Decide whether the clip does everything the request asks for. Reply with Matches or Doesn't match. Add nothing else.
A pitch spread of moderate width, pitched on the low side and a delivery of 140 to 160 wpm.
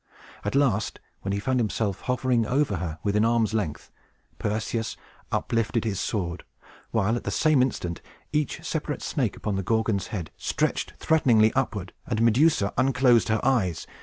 Matches